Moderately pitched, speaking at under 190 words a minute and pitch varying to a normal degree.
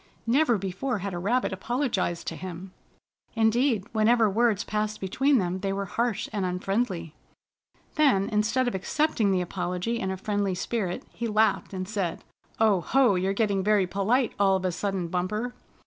No: high, 200 Hz; average, 165 wpm; average, 3.7 semitones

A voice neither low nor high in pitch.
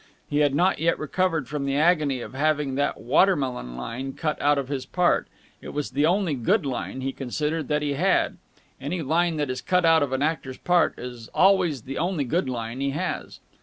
Yes: medium, 145 Hz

